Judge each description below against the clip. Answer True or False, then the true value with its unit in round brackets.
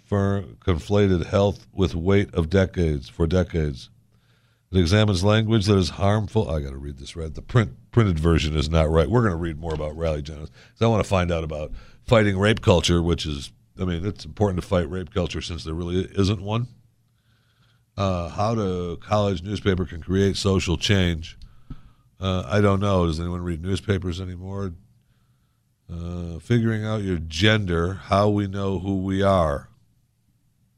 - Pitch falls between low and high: False (95 Hz)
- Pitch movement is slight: False (4.1 semitones)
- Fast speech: False (175 wpm)